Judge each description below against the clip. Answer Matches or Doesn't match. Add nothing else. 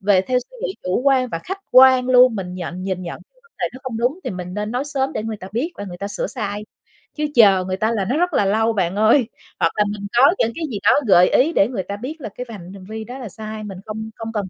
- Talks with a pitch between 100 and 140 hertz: Doesn't match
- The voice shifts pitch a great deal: Doesn't match